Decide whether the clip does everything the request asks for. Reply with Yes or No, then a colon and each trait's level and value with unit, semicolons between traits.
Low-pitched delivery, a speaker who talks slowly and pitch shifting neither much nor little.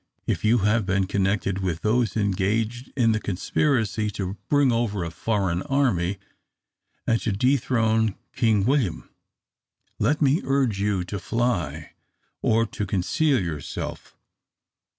Yes: low, 110 Hz; slow, 130 wpm; average, 3.8 semitones